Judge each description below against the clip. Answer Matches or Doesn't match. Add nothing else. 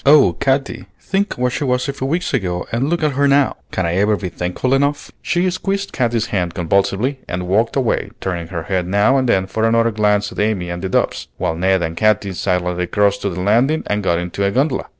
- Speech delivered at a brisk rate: Matches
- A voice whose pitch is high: Doesn't match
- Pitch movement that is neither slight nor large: Doesn't match